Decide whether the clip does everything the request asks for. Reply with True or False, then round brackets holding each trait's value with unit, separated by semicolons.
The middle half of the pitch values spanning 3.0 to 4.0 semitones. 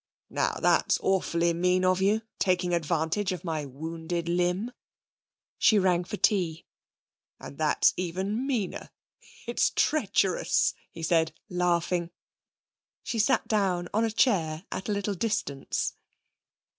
True (3.3 semitones)